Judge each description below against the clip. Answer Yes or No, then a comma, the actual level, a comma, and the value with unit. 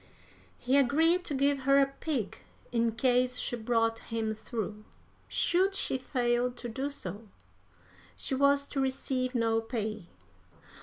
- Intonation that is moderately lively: Yes, average, 3.5 semitones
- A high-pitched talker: Yes, very high, 250 Hz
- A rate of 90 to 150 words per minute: Yes, average, 140 wpm